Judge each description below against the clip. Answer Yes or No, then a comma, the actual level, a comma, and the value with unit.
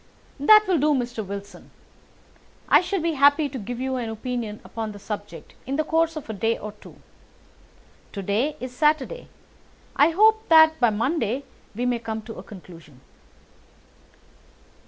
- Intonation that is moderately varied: No, wide, 6.3 semitones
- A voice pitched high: Yes, very high, 250 Hz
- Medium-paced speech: Yes, average, 165 wpm